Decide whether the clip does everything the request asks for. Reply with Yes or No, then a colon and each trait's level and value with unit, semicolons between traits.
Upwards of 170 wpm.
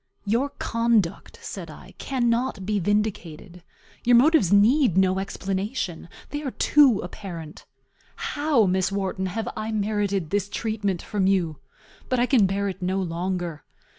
No: average, 140 wpm